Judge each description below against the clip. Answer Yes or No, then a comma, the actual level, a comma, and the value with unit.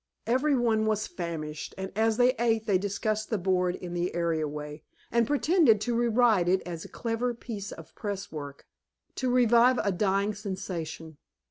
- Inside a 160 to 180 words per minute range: Yes, average, 170 wpm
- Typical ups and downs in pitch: Yes, average, 5.0 semitones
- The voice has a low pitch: No, high, 205 Hz